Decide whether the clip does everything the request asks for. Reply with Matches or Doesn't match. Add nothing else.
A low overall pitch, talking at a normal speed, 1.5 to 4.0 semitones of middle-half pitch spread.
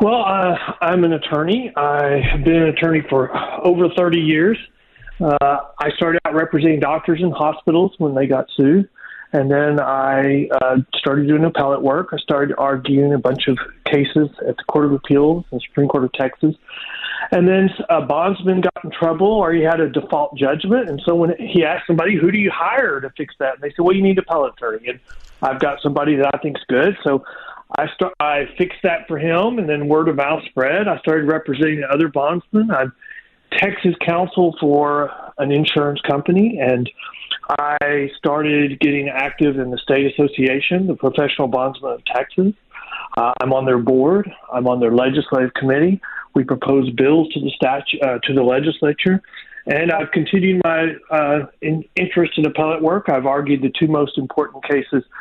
Doesn't match